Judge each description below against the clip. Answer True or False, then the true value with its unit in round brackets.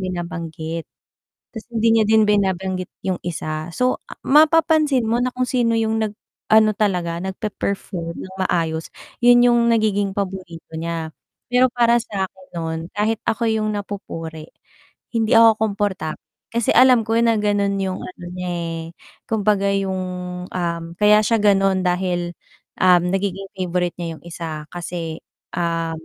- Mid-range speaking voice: False (195 Hz)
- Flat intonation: False (4.2 semitones)